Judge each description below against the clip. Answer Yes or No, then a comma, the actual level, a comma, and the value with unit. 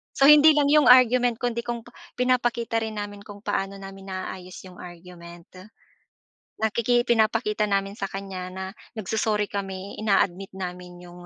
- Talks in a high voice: Yes, high, 205 Hz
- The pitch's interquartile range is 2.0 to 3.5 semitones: No, average, 3.9 semitones